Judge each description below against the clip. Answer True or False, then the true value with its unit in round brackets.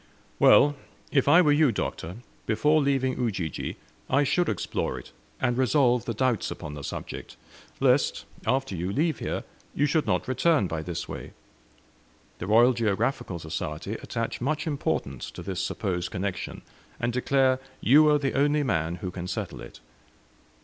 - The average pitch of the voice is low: True (120 Hz)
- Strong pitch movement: True (7.2 semitones)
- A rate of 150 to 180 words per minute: True (155 wpm)